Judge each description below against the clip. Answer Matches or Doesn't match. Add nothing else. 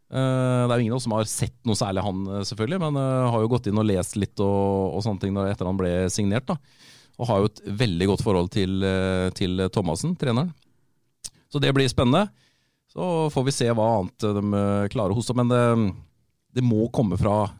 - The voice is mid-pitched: Doesn't match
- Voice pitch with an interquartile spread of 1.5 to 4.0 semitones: Doesn't match